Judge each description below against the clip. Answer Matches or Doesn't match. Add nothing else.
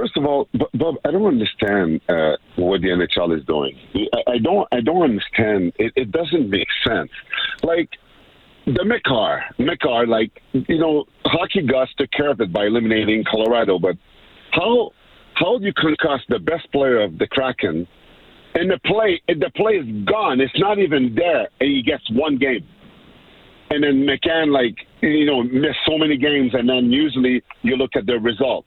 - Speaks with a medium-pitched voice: Doesn't match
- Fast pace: Doesn't match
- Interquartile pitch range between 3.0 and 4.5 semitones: Doesn't match